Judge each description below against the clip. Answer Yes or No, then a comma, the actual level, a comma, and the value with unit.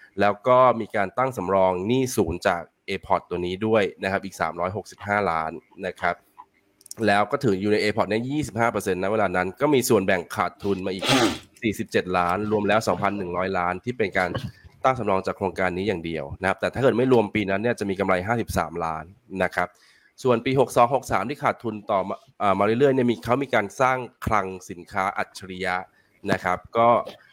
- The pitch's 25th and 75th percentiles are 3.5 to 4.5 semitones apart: Yes, average, 3.9 semitones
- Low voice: Yes, low, 100 Hz